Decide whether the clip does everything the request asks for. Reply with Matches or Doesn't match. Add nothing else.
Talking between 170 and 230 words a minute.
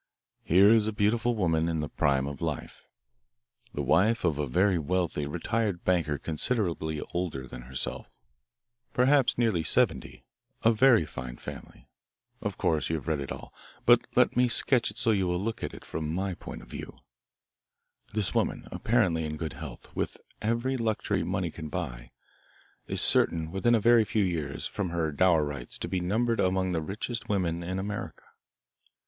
Matches